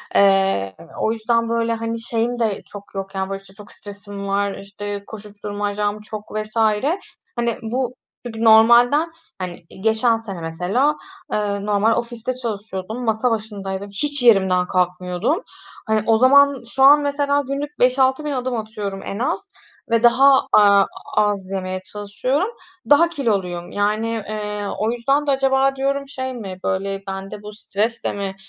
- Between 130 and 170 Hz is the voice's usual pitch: No, high, 220 Hz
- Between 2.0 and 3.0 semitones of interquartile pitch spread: No, average, 3.9 semitones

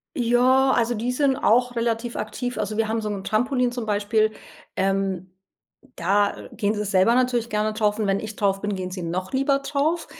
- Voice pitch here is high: Yes, high, 220 Hz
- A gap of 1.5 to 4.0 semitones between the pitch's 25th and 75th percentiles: Yes, average, 3.4 semitones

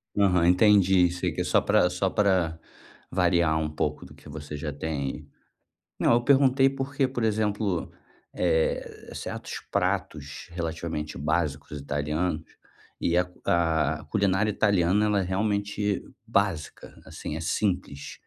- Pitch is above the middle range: No, very low, 90 Hz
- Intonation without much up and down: No, average, 4.6 semitones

